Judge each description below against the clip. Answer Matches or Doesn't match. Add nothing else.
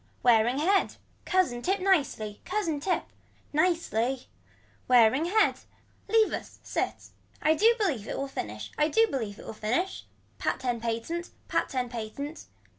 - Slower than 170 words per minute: Matches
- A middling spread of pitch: Doesn't match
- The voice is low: Doesn't match